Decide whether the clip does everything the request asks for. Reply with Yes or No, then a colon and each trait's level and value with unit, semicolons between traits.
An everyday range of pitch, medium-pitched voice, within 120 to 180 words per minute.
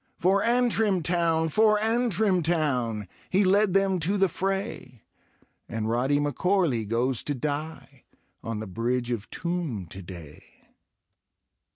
No: wide, 8.4 semitones; medium, 160 Hz; average, 140 wpm